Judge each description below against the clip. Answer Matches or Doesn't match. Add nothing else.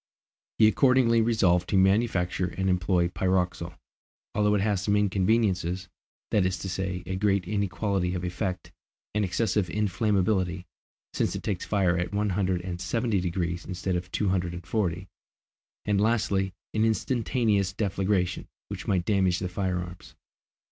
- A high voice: Doesn't match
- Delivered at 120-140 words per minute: Doesn't match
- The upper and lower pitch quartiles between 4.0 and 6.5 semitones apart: Doesn't match